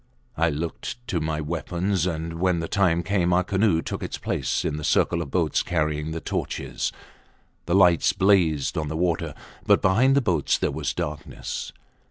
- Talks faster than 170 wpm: Yes, average, 180 wpm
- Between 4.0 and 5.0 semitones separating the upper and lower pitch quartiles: No, average, 2.9 semitones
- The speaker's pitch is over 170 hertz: No, very low, 85 Hz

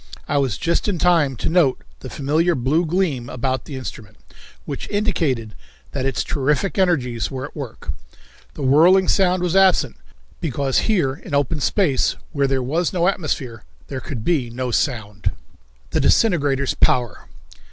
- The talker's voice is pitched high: No, medium, 140 Hz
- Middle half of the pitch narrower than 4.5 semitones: No, average, 5.2 semitones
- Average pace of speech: Yes, average, 155 wpm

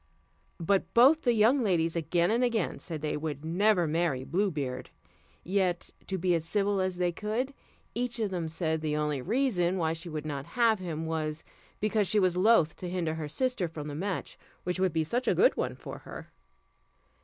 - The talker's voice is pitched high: No, medium, 175 Hz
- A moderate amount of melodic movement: Yes, average, 4.7 semitones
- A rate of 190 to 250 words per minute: Yes, average, 200 wpm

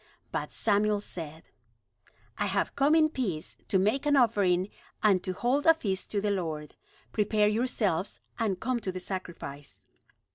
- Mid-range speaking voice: No, high, 205 Hz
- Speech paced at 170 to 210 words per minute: No, average, 155 wpm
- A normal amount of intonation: Yes, average, 4.2 semitones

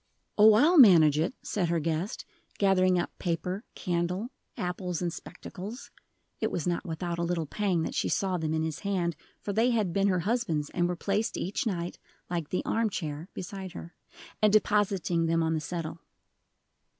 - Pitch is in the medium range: Yes, medium, 180 Hz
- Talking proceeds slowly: No, average, 180 wpm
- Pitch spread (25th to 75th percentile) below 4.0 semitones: Yes, average, 3.3 semitones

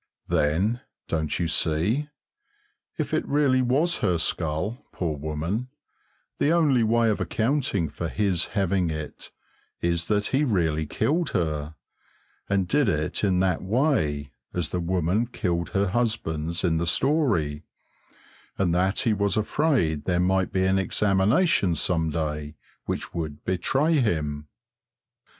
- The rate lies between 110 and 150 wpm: Yes, slow, 135 wpm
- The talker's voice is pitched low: Yes, very low, 95 Hz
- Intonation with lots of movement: Yes, wide, 6.2 semitones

